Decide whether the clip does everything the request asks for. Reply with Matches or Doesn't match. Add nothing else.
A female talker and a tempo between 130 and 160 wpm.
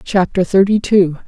Matches